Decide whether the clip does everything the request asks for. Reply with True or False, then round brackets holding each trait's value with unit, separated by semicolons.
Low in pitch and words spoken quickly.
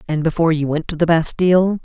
False (165 Hz; 230 wpm)